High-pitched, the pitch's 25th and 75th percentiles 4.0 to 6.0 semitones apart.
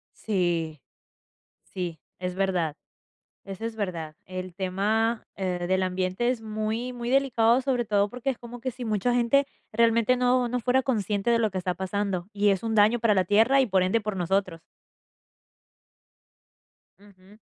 Yes: high, 210 Hz; average, 4.3 semitones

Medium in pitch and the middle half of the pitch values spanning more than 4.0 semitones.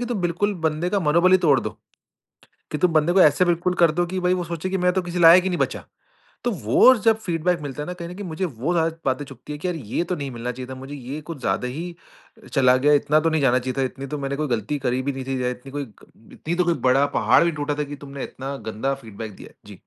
Yes: medium, 150 Hz; average, 4.7 semitones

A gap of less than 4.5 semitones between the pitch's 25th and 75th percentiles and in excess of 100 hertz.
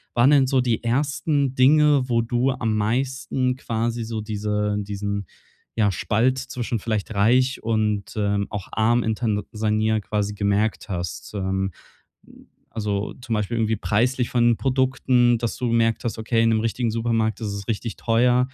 Yes: average, 2.9 semitones; low, 115 Hz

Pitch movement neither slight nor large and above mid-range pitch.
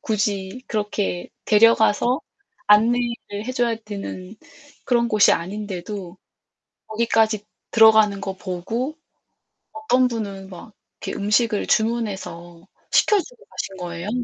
Yes: average, 3.2 semitones; high, 210 Hz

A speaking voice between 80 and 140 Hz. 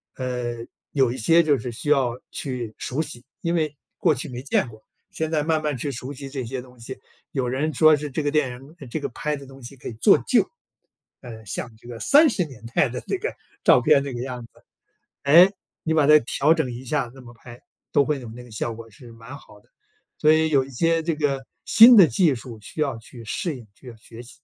Yes: low, 135 Hz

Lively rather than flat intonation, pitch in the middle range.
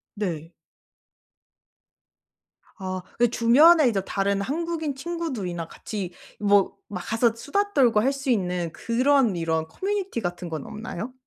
No: wide, 7.1 semitones; high, 225 Hz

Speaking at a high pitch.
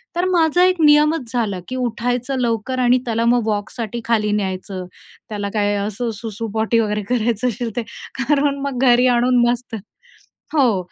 Yes: high, 235 Hz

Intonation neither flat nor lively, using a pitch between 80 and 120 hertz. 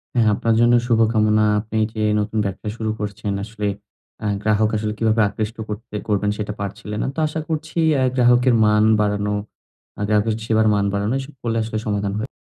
No: narrow, 1.6 semitones; low, 110 Hz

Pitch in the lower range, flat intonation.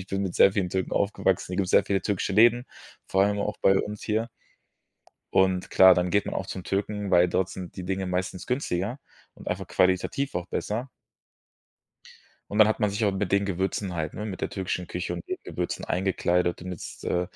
Yes: very low, 95 Hz; narrow, 2.2 semitones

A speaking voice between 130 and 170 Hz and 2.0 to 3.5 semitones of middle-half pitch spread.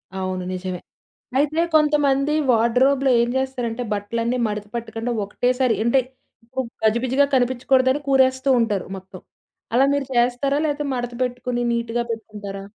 No: high, 245 Hz; average, 2.9 semitones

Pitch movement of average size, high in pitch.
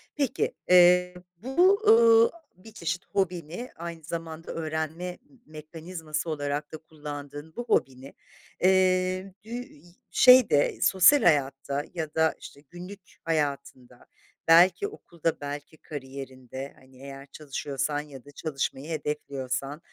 No: average, 4.2 semitones; medium, 160 Hz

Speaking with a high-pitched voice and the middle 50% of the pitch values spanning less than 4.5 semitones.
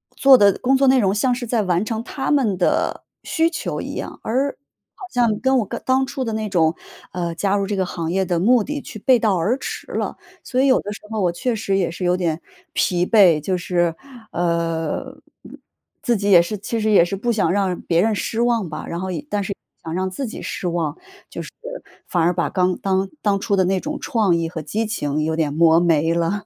No: high, 195 Hz; average, 4.8 semitones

